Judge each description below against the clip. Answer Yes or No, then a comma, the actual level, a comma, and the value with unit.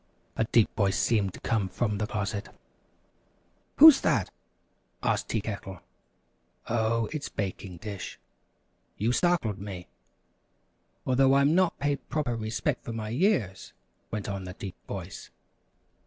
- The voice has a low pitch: Yes, low, 110 Hz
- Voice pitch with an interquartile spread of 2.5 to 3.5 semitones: No, average, 4.7 semitones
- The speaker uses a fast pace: No, slow, 135 wpm